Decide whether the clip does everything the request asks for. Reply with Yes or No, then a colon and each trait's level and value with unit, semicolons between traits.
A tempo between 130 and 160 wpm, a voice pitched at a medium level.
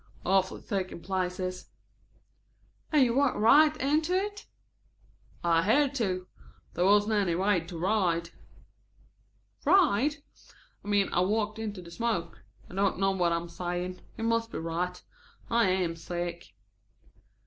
No: average, 140 wpm; high, 195 Hz